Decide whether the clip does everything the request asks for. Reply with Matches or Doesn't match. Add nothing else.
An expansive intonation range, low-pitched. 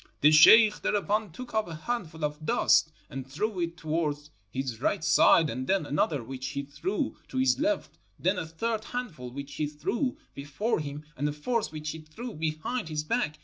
Doesn't match